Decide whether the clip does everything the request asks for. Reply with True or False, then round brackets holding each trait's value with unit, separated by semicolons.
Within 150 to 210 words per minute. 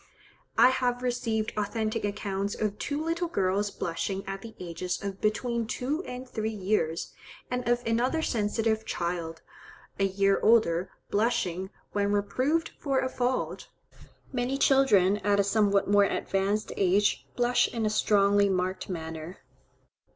False (140 wpm)